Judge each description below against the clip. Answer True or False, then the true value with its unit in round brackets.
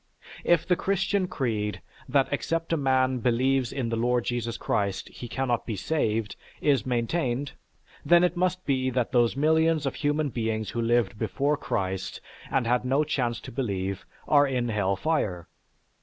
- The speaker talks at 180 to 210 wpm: False (165 wpm)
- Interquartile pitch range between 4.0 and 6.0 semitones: True (4.3 semitones)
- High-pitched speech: False (130 Hz)